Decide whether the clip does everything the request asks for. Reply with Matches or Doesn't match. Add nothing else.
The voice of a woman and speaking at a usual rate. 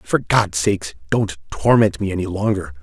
Doesn't match